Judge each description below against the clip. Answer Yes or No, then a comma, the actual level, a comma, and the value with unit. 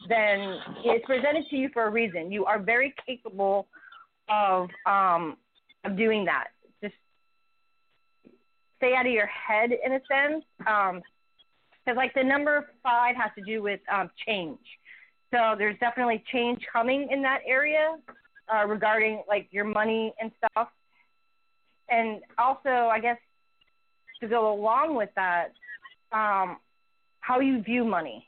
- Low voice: No, high, 235 Hz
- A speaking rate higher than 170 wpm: No, average, 140 wpm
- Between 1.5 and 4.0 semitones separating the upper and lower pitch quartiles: No, average, 4.6 semitones